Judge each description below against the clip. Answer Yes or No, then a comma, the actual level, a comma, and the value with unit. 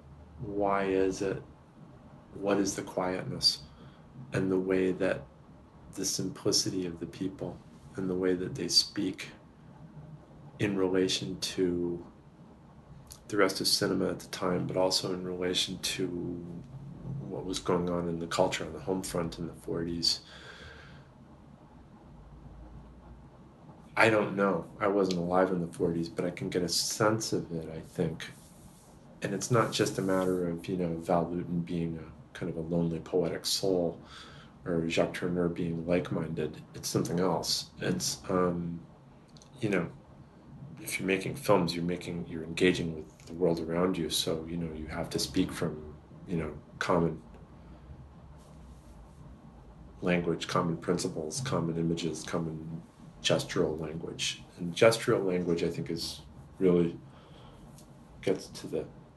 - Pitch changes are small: Yes, narrow, 2.1 semitones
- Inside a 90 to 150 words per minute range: Yes, average, 145 wpm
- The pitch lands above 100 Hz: No, very low, 85 Hz